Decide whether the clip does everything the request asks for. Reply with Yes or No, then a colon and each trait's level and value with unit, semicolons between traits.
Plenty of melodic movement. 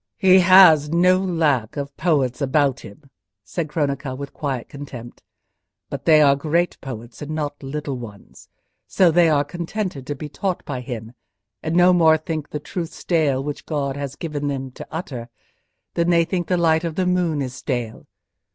No: average, 3.7 semitones